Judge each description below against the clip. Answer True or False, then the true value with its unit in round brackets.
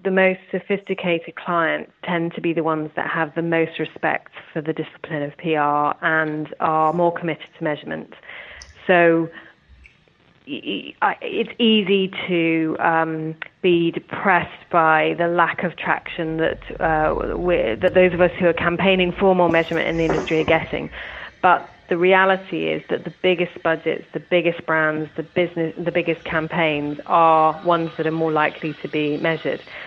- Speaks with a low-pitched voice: False (165 Hz)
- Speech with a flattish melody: True (1.8 semitones)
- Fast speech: False (160 wpm)